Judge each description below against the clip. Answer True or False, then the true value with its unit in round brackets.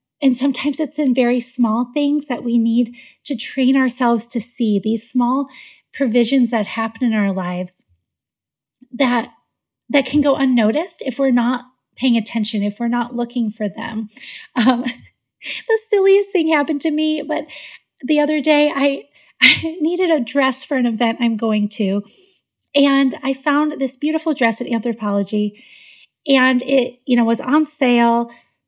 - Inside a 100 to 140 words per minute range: False (160 wpm)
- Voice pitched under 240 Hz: False (255 Hz)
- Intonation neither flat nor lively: True (3.7 semitones)